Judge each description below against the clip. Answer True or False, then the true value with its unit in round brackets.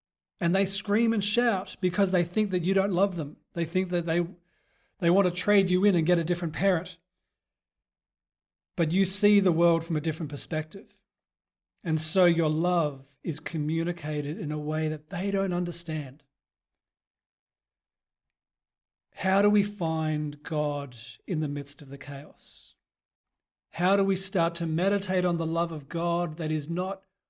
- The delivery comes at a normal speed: True (165 wpm)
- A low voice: False (170 Hz)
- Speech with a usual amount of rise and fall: True (3.4 semitones)